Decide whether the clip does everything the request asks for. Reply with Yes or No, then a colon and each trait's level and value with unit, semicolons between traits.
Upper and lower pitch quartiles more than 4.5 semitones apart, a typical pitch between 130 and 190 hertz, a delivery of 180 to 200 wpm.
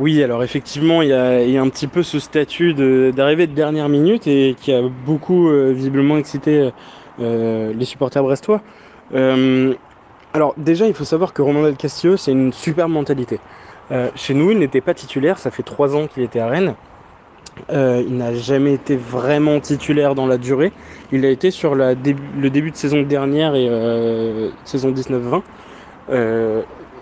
No: average, 2.7 semitones; medium, 140 Hz; average, 185 wpm